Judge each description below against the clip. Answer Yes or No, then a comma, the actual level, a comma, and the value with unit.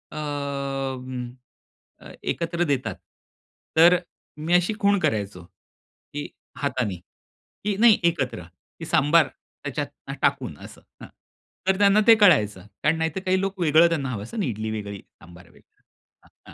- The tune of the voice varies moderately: No, wide, 7.2 semitones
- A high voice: No, medium, 145 Hz